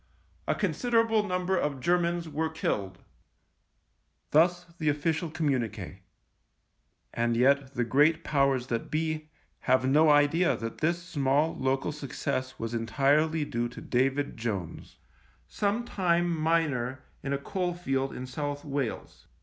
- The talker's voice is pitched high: No, medium, 145 Hz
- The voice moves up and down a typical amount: Yes, average, 4.2 semitones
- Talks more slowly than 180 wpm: Yes, slow, 135 wpm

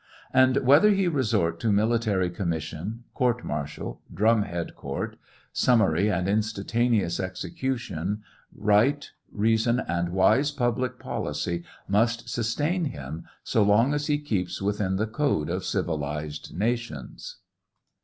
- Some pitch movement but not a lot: No, wide, 5.7 semitones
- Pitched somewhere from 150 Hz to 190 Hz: No, low, 105 Hz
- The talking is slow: Yes, slow, 120 wpm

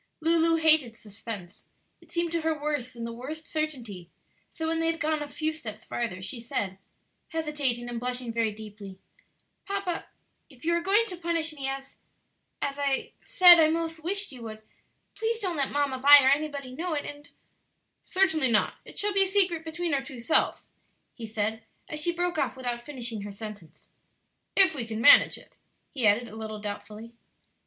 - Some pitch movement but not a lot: No, wide, 6.0 semitones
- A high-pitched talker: Yes, very high, 285 Hz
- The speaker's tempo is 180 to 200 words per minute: Yes, average, 190 wpm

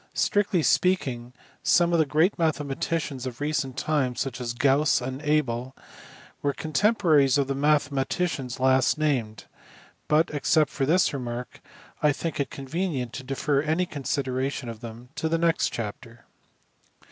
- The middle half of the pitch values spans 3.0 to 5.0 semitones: Yes, average, 3.3 semitones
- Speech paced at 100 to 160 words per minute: Yes, average, 150 wpm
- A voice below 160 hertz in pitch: Yes, medium, 140 Hz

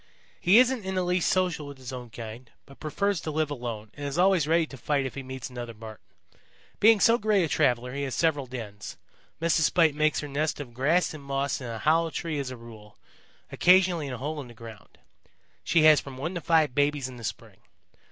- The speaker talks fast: Yes, fast, 225 wpm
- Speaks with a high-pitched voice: No, medium, 145 Hz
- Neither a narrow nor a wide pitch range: Yes, average, 4.7 semitones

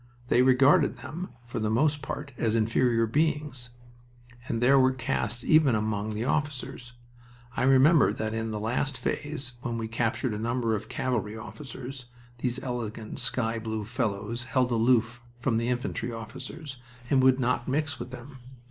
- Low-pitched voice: Yes, low, 120 Hz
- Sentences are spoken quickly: No, average, 160 wpm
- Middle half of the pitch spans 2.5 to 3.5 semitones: Yes, average, 2.8 semitones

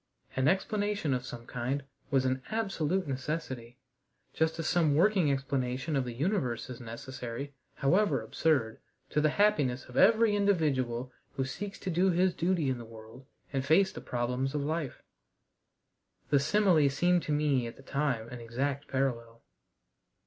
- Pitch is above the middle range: No, medium, 140 Hz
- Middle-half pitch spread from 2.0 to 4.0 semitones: No, average, 5.2 semitones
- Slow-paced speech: No, average, 155 wpm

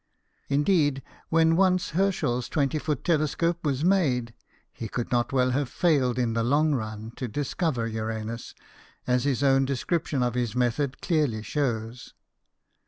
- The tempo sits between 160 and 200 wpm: No, average, 145 wpm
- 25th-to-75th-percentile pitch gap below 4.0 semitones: No, average, 4.3 semitones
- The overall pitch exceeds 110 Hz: Yes, low, 135 Hz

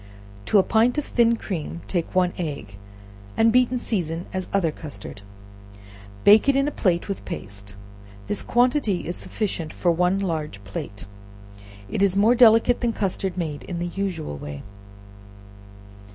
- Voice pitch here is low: No, medium, 185 Hz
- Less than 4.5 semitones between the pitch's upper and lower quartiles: No, wide, 5.6 semitones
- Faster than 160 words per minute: No, average, 155 wpm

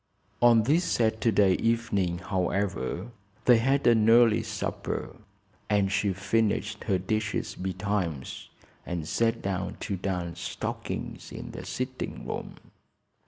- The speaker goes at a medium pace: No, slow, 120 wpm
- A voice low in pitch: Yes, low, 105 Hz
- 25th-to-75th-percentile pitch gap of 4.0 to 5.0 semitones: No, average, 3.5 semitones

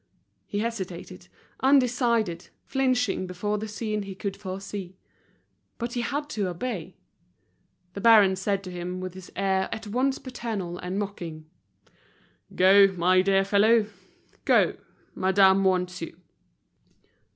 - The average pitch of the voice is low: No, high, 195 Hz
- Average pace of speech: No, slow, 125 wpm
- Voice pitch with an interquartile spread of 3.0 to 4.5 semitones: Yes, average, 3.5 semitones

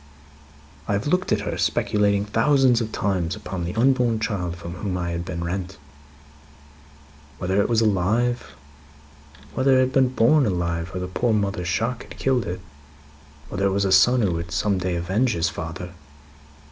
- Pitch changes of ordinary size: Yes, average, 4.7 semitones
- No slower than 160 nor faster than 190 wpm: Yes, average, 175 wpm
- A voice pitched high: No, low, 100 Hz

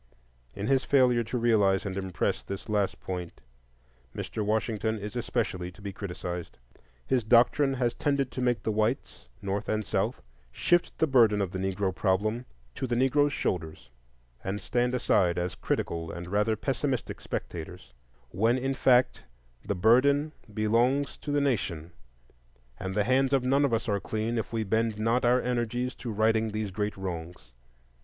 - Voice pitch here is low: Yes, low, 110 Hz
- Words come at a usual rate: Yes, average, 165 wpm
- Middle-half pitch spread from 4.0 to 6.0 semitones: Yes, average, 4.3 semitones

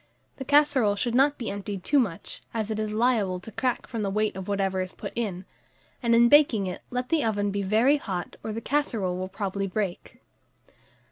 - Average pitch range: Yes, average, 4.0 semitones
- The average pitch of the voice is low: No, high, 215 Hz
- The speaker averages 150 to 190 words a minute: No, fast, 205 wpm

